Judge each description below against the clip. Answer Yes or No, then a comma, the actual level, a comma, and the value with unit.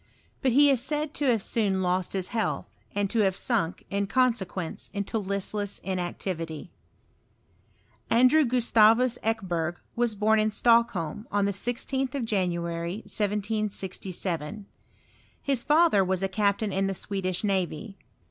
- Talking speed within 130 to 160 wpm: Yes, slow, 135 wpm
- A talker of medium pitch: No, high, 205 Hz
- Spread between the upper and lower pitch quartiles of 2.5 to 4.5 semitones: Yes, average, 3.8 semitones